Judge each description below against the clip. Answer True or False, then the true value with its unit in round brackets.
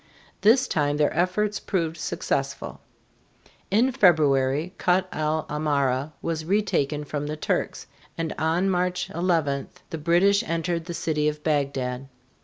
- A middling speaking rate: False (130 wpm)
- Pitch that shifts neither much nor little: True (3.5 semitones)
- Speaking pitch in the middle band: True (160 Hz)